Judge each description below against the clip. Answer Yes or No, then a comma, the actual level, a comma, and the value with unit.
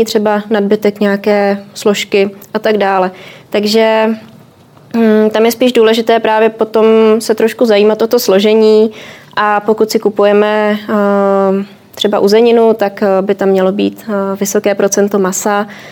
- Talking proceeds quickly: No, average, 130 wpm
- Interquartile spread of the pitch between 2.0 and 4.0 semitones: No, narrow, 1.6 semitones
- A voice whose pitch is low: No, high, 210 Hz